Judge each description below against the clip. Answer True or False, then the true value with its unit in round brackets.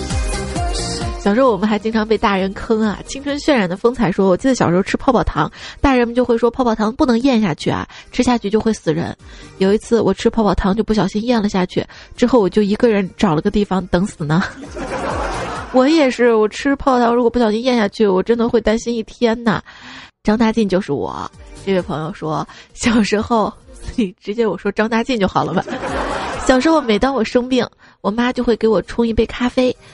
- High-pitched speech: True (220 Hz)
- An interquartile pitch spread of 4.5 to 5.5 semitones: False (3.2 semitones)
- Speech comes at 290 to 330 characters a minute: True (310 characters per minute)